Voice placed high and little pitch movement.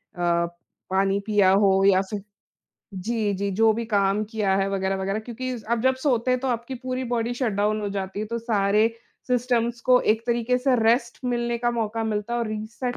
No: high, 220 Hz; average, 3.1 semitones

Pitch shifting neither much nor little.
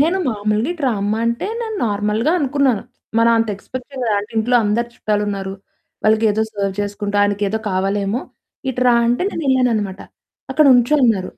Yes: average, 3.5 semitones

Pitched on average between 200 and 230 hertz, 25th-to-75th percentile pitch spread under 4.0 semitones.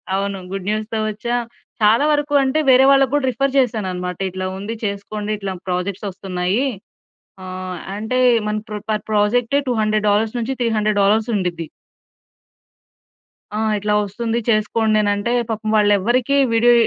Yes: high, 215 Hz; average, 2.8 semitones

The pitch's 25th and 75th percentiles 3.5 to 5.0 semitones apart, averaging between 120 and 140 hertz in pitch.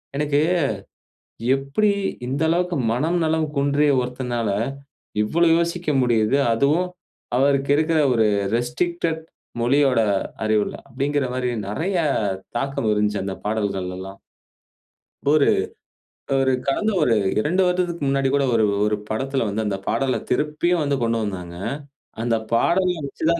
No: wide, 5.6 semitones; low, 135 Hz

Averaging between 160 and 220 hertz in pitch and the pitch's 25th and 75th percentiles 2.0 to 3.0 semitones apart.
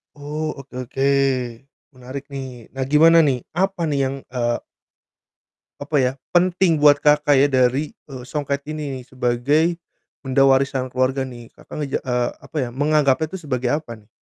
No: low, 135 Hz; narrow, 2.6 semitones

